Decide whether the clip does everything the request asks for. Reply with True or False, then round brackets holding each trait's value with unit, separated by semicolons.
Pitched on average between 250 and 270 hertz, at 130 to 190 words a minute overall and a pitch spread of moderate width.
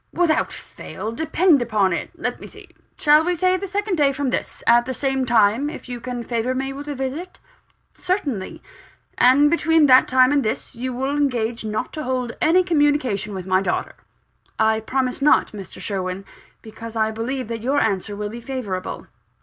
True (255 Hz; 185 wpm; 4.8 semitones)